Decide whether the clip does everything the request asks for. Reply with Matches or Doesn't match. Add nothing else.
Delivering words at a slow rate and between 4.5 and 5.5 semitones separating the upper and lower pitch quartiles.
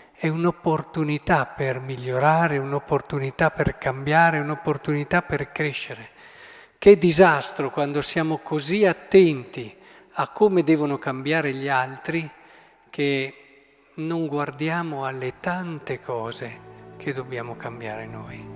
Doesn't match